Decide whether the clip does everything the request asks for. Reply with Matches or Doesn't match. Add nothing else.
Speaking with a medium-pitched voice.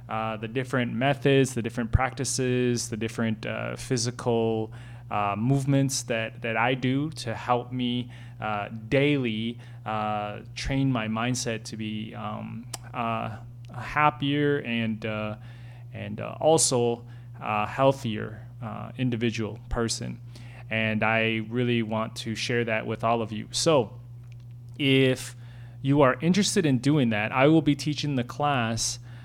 Doesn't match